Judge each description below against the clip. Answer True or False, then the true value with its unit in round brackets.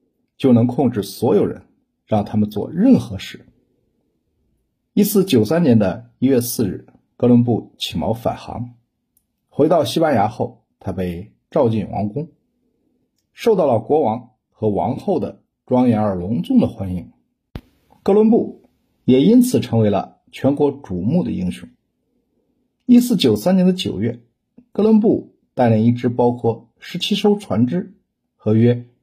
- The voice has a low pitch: True (120 Hz)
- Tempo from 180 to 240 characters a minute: True (205 characters per minute)